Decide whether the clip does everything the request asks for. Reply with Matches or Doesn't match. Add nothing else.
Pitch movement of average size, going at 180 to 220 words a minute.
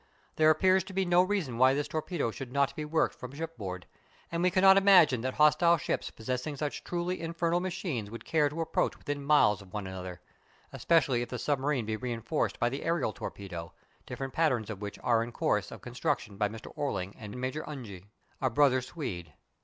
Doesn't match